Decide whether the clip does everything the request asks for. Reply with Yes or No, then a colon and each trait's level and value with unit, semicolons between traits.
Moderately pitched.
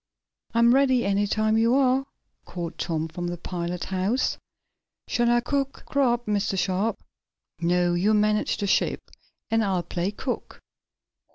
No: high, 210 Hz